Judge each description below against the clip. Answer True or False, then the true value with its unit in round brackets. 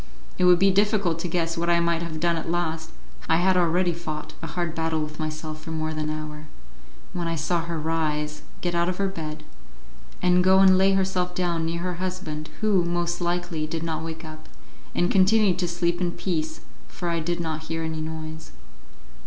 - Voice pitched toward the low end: False (170 Hz)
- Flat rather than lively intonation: True (2.1 semitones)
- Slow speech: False (205 wpm)